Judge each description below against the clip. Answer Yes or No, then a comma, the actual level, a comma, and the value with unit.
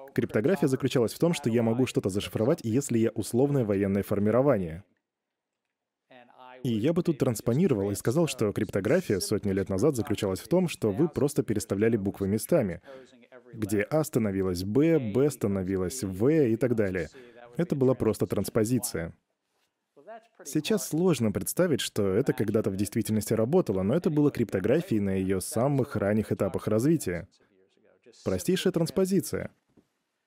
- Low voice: Yes, low, 115 Hz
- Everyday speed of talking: Yes, average, 140 wpm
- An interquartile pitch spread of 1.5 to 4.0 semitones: No, wide, 5.5 semitones